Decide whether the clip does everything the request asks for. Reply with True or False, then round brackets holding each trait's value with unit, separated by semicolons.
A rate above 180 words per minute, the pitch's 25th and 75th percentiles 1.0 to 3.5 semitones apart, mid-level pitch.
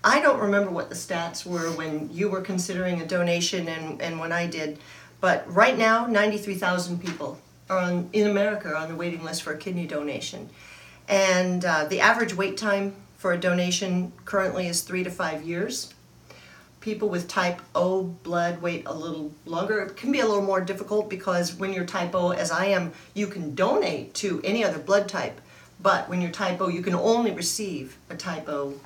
True (200 wpm; 2.9 semitones; 180 Hz)